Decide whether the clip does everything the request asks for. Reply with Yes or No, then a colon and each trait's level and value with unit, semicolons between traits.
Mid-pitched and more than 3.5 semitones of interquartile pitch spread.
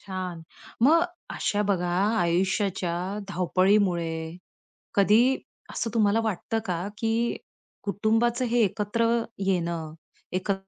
No: high, 195 Hz; average, 4.1 semitones